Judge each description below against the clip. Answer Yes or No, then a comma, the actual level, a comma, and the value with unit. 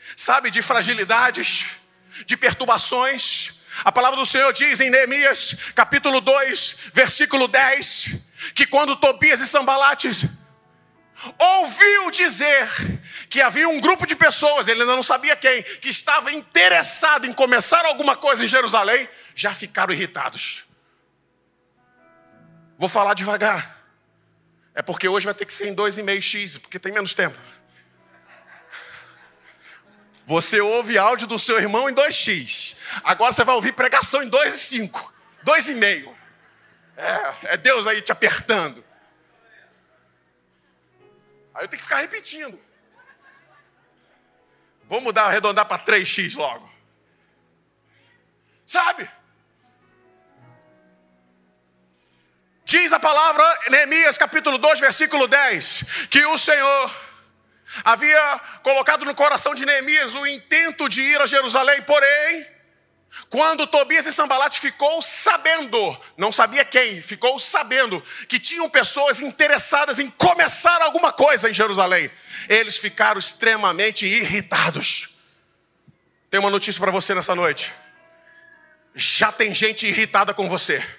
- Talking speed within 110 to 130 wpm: Yes, slow, 120 wpm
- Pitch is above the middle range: Yes, very high, 265 Hz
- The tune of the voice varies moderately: No, wide, 6.2 semitones